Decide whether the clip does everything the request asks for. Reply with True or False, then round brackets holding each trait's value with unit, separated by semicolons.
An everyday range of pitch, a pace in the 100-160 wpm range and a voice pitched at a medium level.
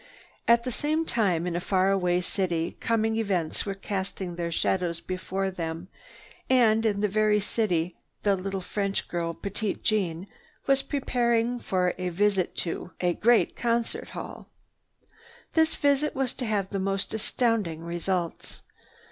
False (4.1 semitones; 150 wpm; 195 Hz)